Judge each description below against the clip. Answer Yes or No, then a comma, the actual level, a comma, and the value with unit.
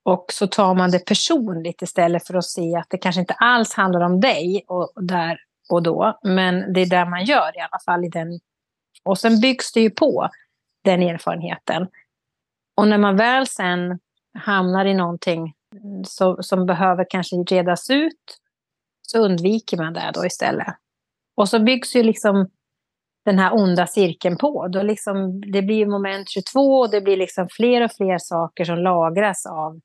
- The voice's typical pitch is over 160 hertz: Yes, high, 190 Hz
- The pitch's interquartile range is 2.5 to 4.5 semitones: Yes, average, 2.9 semitones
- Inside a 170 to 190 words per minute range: Yes, average, 175 wpm